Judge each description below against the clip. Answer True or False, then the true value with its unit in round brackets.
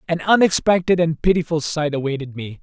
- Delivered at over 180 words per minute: False (160 wpm)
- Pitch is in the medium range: True (160 Hz)